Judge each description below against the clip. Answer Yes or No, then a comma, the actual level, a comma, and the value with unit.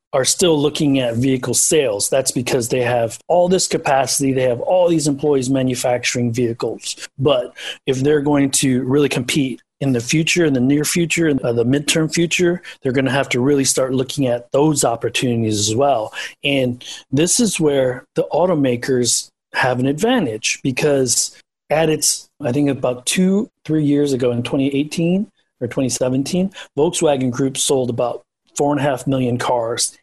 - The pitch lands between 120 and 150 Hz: Yes, low, 135 Hz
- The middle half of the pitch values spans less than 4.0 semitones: Yes, average, 3.5 semitones